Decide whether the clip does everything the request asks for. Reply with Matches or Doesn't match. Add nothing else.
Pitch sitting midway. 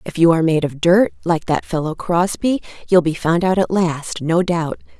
Matches